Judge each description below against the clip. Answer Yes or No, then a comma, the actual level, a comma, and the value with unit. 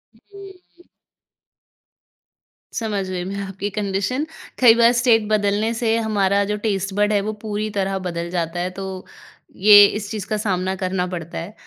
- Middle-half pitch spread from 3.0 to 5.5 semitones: No, narrow, 2.6 semitones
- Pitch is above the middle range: Yes, high, 205 Hz